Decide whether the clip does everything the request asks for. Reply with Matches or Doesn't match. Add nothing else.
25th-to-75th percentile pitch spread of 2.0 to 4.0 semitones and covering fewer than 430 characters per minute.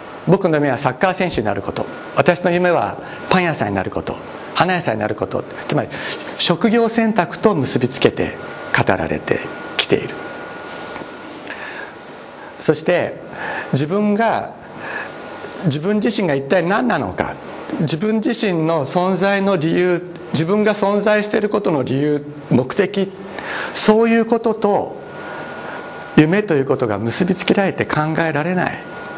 Doesn't match